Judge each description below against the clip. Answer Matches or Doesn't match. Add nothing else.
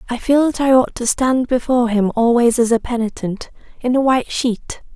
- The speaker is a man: Doesn't match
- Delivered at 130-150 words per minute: Doesn't match